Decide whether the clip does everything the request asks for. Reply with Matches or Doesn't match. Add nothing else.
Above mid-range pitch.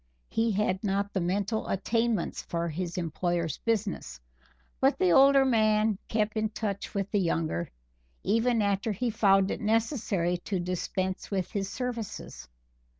Matches